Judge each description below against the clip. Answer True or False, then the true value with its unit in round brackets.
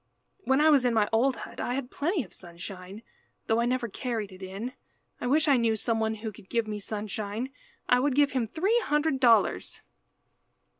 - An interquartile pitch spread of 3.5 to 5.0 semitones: True (4.2 semitones)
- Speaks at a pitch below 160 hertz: False (235 Hz)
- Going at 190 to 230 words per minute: True (200 wpm)